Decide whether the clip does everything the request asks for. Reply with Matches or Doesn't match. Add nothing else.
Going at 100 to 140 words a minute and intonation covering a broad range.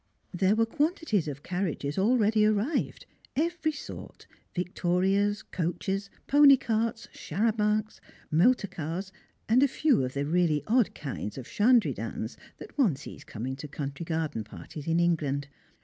Matches